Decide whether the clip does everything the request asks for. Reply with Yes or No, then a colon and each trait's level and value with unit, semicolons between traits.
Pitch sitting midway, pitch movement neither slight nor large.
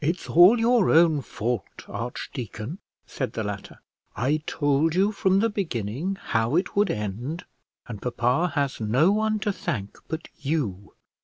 No: medium, 145 Hz; wide, 8.1 semitones